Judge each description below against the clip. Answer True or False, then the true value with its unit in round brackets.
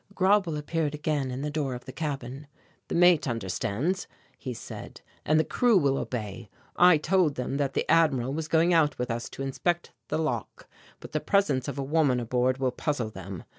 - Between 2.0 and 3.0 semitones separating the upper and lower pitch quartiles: False (4.2 semitones)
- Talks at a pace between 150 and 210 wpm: True (195 wpm)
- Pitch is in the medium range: True (145 Hz)